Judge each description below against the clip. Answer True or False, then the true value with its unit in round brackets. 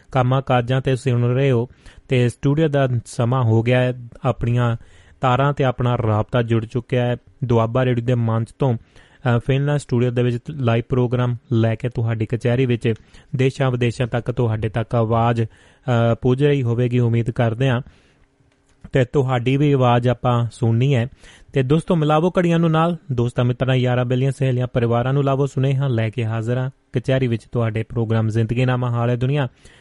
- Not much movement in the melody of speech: True (2.2 semitones)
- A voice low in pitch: True (125 Hz)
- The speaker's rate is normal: False (170 wpm)